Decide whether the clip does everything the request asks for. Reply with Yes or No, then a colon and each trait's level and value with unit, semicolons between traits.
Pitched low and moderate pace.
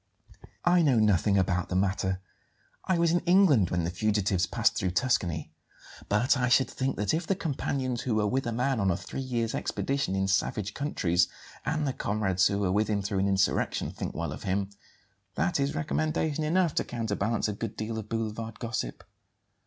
Yes: low, 110 Hz; average, 190 wpm